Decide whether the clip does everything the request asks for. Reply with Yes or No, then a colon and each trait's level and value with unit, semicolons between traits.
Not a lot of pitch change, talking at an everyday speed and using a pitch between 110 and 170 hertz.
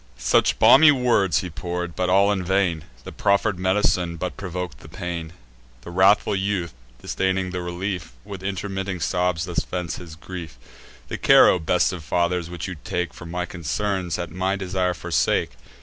No: narrow, 1.8 semitones; average, 170 wpm; very low, 90 Hz